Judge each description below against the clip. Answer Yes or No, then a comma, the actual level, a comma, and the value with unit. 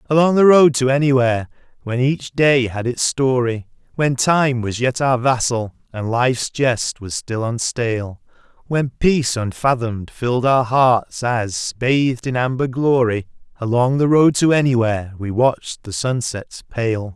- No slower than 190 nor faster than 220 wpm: No, average, 155 wpm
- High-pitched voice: No, low, 125 Hz